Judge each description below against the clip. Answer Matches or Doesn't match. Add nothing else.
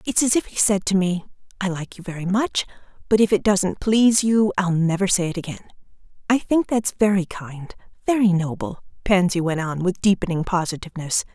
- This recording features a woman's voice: Matches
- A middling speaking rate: Matches